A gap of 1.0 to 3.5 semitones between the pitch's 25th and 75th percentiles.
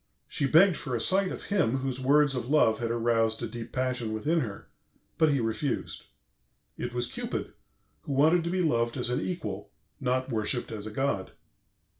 No: average, 4.6 semitones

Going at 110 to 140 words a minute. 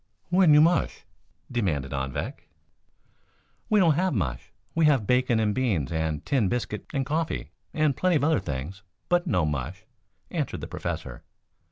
No: average, 155 wpm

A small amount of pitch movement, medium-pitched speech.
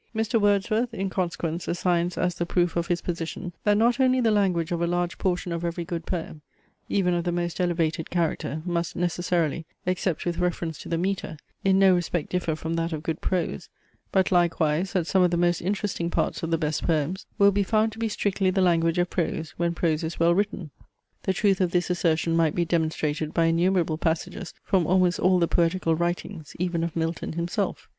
Yes: narrow, 2.0 semitones; medium, 175 Hz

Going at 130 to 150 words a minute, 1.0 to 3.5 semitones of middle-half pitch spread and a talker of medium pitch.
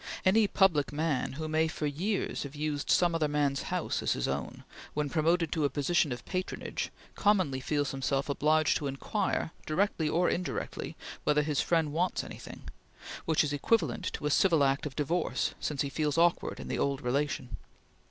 No: average, 180 wpm; average, 2.9 semitones; medium, 150 Hz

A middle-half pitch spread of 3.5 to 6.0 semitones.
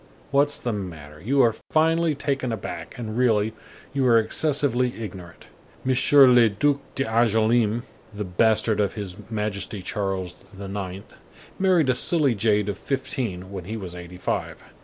Yes: average, 4.9 semitones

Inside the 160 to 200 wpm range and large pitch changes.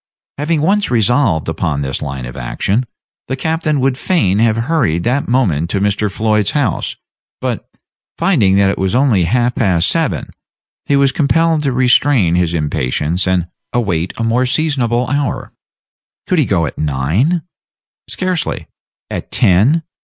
No: average, 150 wpm; wide, 8.2 semitones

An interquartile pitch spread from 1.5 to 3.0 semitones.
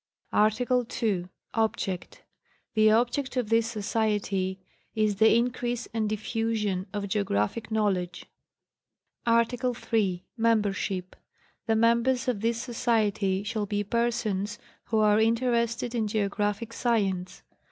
Yes: narrow, 2.4 semitones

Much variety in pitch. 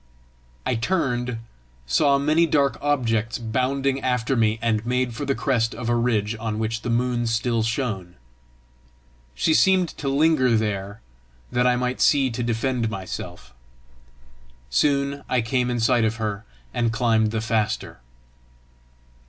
No: average, 3.0 semitones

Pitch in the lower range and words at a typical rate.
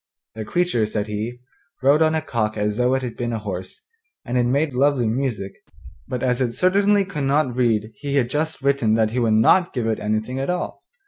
No: low, 125 Hz; fast, 215 wpm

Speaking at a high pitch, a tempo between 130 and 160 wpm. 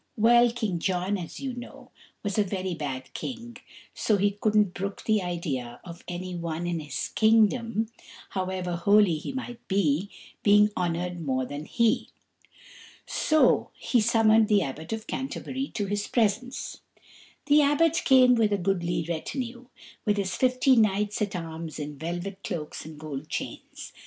Yes: high, 200 Hz; average, 155 wpm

